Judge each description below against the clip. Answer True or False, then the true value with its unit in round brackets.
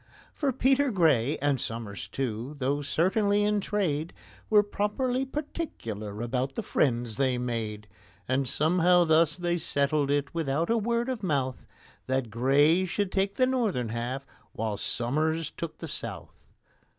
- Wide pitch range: True (8.0 semitones)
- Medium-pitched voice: True (150 Hz)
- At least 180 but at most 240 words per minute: False (145 wpm)